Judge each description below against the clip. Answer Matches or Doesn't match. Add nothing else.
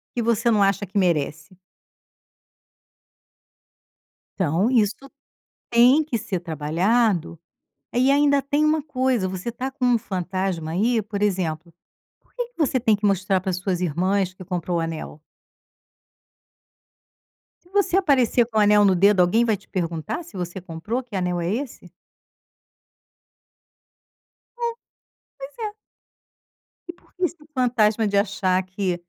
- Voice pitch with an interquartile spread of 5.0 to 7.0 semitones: Matches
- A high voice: Matches